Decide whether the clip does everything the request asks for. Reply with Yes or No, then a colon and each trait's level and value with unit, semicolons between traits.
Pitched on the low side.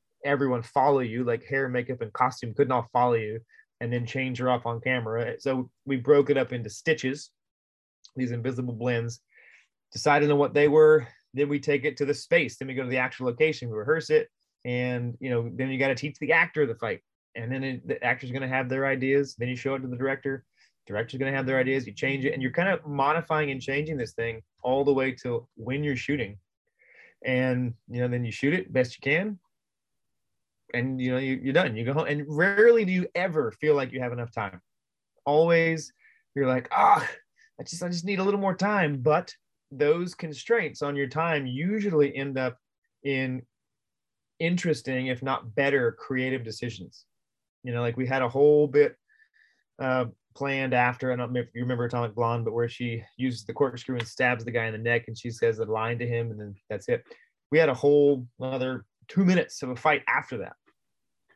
Yes: low, 130 Hz